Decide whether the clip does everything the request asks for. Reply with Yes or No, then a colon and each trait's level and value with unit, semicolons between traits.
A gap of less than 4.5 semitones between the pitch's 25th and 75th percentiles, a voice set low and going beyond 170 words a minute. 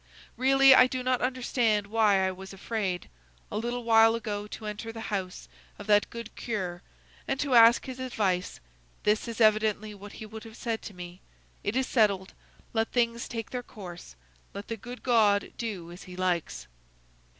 No: average, 2.9 semitones; high, 220 Hz; average, 180 wpm